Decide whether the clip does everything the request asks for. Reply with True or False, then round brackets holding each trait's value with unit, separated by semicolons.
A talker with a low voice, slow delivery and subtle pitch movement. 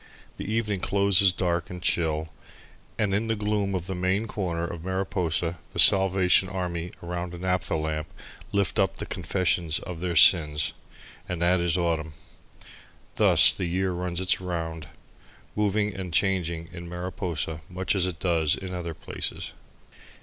False (90 Hz; 155 wpm; 2.1 semitones)